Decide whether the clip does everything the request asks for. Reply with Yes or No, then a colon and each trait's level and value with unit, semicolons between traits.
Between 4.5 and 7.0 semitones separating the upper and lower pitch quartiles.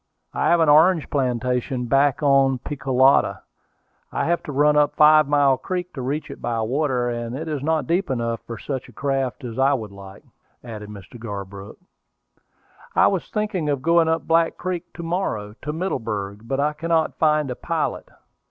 Yes: average, 4.8 semitones